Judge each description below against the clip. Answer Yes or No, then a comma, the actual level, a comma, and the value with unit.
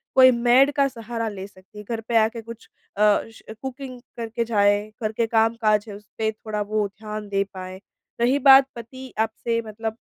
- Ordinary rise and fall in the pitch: No, narrow, 2.1 semitones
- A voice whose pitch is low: No, high, 225 Hz